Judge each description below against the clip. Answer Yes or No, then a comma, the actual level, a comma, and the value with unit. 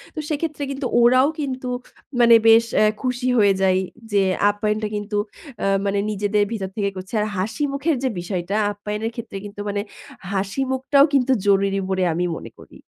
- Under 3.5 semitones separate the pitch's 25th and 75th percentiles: No, average, 4.5 semitones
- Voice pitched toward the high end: Yes, high, 215 Hz